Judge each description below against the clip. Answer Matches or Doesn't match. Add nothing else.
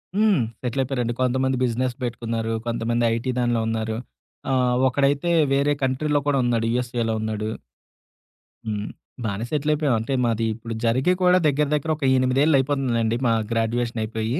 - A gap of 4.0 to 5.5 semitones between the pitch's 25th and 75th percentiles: Doesn't match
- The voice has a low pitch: Matches